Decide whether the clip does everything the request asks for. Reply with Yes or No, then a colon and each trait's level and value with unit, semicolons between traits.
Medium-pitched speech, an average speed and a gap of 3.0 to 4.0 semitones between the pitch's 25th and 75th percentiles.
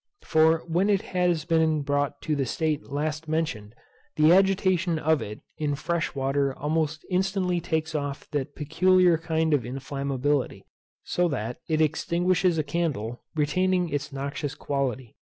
Yes: medium, 155 Hz; average, 145 wpm; average, 3.3 semitones